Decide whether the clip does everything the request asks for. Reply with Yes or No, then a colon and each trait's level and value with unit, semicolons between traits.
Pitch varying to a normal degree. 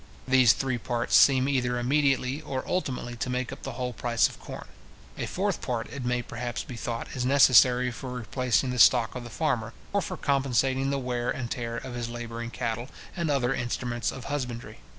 No: narrow, 1.9 semitones